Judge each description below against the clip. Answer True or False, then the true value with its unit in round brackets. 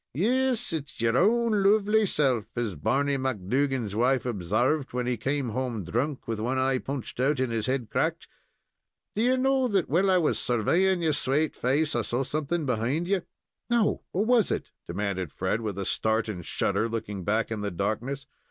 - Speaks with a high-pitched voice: False (130 Hz)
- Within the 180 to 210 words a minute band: True (185 wpm)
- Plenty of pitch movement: True (7.0 semitones)